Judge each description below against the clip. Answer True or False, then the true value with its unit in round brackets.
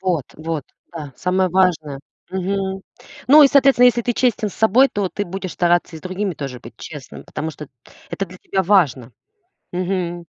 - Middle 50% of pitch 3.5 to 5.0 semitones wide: True (3.8 semitones)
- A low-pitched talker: False (185 Hz)